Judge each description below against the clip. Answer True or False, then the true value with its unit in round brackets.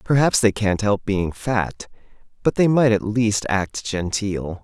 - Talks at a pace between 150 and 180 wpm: True (170 wpm)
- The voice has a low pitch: True (105 Hz)